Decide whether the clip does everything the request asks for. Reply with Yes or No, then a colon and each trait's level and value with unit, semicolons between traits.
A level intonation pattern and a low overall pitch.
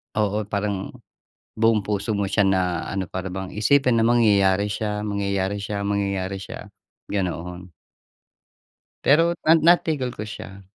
Yes: narrow, 2.0 semitones; low, 100 Hz